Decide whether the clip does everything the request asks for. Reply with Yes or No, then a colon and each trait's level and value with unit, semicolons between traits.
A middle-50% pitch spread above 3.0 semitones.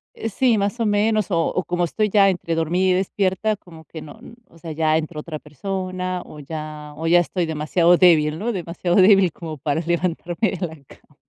Yes: average, 3.4 semitones